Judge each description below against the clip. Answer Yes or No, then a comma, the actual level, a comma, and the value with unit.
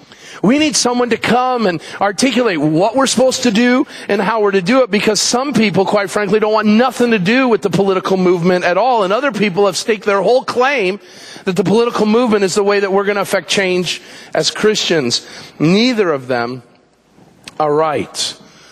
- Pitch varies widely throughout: No, average, 4.1 semitones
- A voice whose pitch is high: Yes, high, 205 Hz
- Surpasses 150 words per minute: Yes, average, 200 wpm